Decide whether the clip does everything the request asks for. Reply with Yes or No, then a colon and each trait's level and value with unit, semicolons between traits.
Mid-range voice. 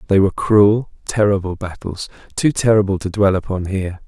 No: low, 100 Hz